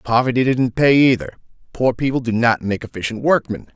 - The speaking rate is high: No, average, 175 wpm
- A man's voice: Yes, male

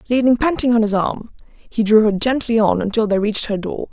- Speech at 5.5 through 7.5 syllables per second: Yes, 5.6 syllables/s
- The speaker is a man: No, female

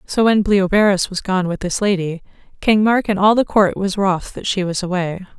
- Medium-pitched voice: No, high, 195 Hz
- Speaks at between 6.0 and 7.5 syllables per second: No, 5.1 syllables/s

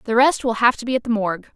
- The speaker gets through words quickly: Yes, fast, 350 wpm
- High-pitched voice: Yes, high, 235 Hz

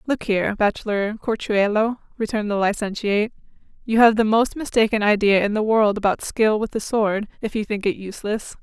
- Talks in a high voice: Yes, high, 215 Hz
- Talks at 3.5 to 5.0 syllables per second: No, 5.5 syllables/s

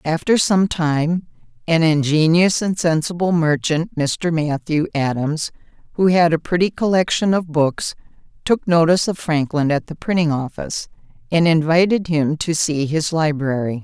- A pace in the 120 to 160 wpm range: Yes, average, 145 wpm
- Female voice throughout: Yes, female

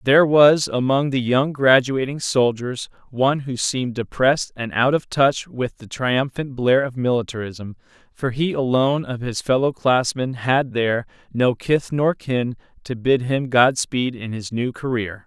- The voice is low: Yes, low, 125 Hz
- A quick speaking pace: No, average, 170 wpm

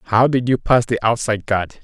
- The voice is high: No, low, 115 Hz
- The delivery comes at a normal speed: No, fast, 230 wpm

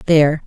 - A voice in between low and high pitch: Yes, medium, 150 Hz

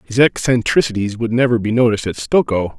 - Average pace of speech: Yes, average, 170 wpm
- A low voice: Yes, low, 115 Hz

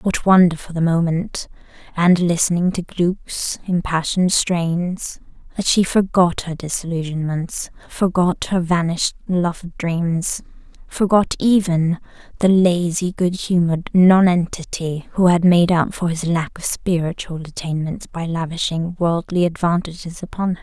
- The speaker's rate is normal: No, slow, 130 wpm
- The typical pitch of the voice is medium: Yes, medium, 175 Hz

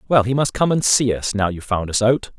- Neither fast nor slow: No, fast, 300 wpm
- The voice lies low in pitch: Yes, low, 115 Hz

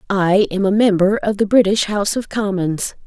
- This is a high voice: Yes, high, 200 Hz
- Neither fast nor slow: Yes, average, 195 wpm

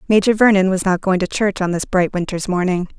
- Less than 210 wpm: No, fast, 240 wpm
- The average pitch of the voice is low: No, high, 190 Hz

